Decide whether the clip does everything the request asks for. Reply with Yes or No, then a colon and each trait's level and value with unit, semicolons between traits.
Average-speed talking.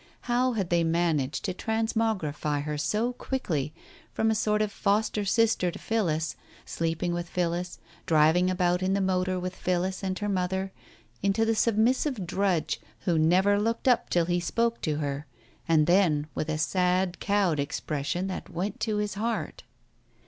Yes: average, 165 wpm